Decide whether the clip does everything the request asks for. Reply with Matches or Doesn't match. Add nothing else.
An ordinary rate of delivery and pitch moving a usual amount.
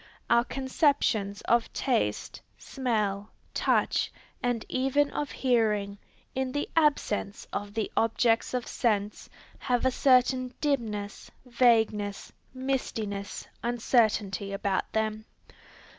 Doesn't match